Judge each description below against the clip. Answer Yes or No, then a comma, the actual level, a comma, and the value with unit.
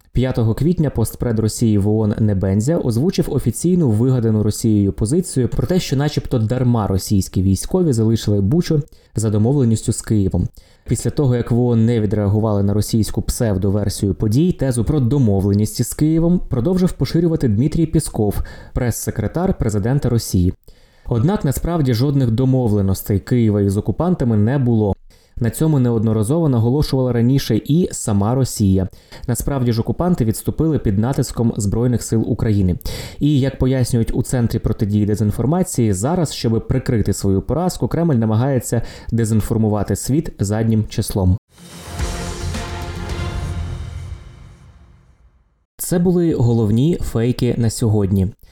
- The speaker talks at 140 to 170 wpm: No, average, 120 wpm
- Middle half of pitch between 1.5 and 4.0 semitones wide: No, average, 4.4 semitones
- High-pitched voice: No, low, 115 Hz